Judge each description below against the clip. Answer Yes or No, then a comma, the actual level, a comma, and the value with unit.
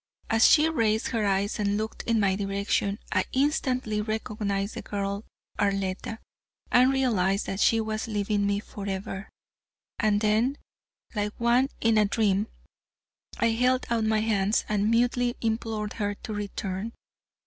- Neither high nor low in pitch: No, high, 215 Hz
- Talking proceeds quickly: No, average, 145 wpm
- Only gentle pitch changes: Yes, narrow, 2.3 semitones